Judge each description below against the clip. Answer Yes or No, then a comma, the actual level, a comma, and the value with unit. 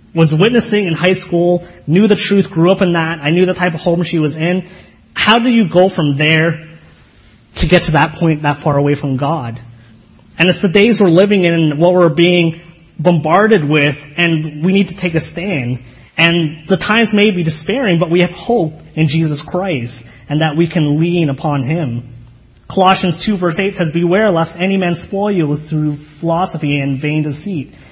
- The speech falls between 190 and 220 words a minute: Yes, average, 200 wpm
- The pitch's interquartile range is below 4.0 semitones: Yes, average, 3.4 semitones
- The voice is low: No, medium, 170 Hz